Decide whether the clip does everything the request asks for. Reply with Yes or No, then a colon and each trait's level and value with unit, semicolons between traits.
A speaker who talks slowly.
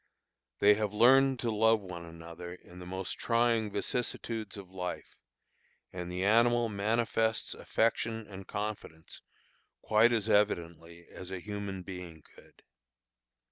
Yes: slow, 130 wpm